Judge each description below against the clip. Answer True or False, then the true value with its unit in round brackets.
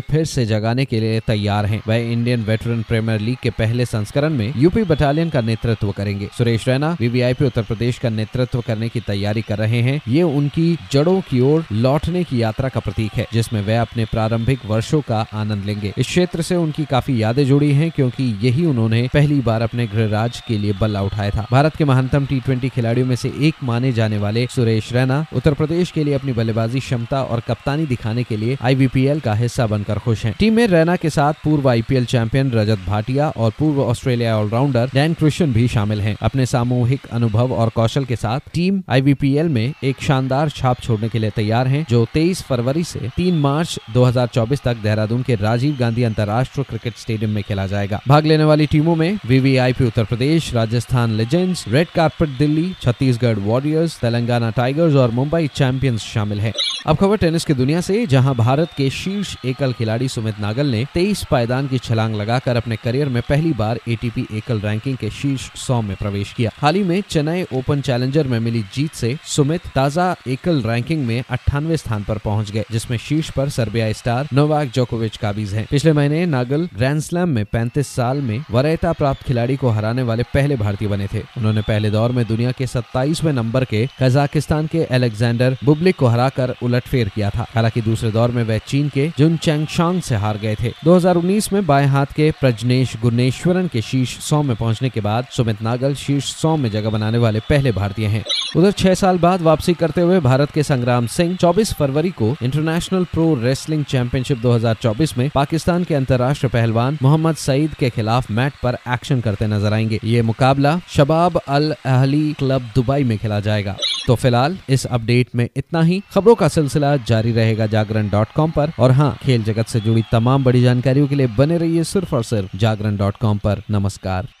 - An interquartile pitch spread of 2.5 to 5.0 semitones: True (4.5 semitones)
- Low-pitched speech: True (125 Hz)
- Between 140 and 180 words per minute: False (190 wpm)